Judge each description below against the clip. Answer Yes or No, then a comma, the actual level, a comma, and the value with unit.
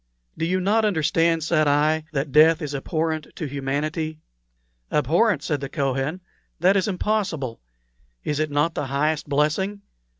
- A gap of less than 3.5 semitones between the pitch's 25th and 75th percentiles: Yes, average, 2.7 semitones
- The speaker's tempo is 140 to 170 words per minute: Yes, average, 145 wpm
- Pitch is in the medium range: Yes, medium, 155 Hz